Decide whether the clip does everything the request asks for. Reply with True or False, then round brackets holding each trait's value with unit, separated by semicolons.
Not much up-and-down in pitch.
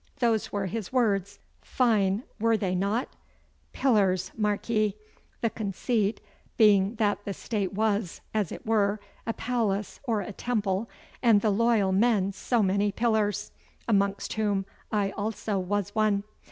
True (2.1 semitones)